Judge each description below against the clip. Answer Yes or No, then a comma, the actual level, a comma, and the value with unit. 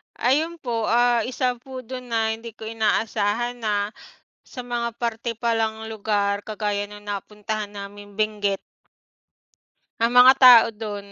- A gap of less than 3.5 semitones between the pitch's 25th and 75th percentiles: Yes, narrow, 2.6 semitones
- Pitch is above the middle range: Yes, high, 220 Hz